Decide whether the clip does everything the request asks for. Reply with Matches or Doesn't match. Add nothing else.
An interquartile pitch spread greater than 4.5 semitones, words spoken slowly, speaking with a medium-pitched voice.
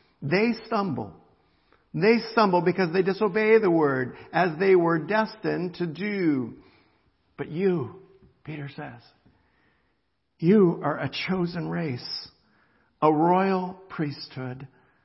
Matches